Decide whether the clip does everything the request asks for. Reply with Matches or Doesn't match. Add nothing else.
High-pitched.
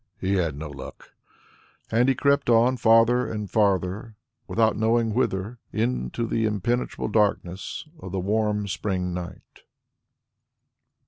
Doesn't match